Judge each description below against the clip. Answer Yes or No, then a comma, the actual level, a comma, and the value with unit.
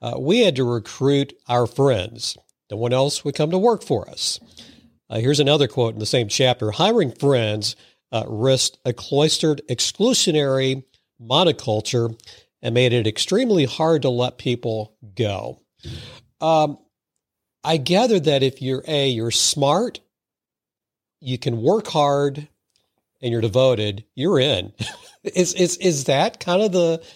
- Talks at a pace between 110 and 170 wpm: Yes, average, 145 wpm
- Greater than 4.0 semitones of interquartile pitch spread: Yes, average, 4.5 semitones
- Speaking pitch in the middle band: No, low, 130 Hz